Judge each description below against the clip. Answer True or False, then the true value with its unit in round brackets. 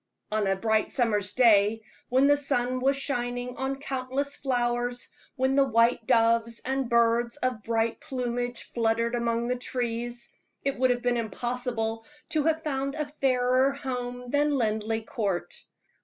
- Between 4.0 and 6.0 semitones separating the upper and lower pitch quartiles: False (2.5 semitones)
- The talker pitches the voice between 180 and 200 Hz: False (245 Hz)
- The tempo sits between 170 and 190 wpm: False (150 wpm)